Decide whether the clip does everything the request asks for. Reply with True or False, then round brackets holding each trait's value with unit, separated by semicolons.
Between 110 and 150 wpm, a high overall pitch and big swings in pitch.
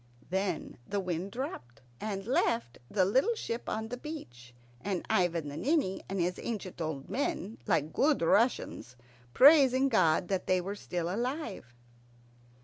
True (145 wpm; 195 Hz; 6.4 semitones)